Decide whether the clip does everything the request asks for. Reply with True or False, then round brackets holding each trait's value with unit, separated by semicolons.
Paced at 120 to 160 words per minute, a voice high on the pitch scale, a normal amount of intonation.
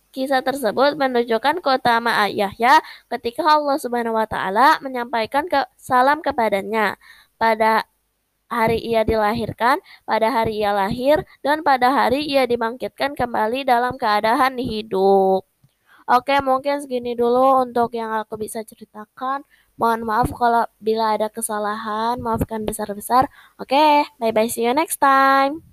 True (135 wpm; 235 Hz; 3.4 semitones)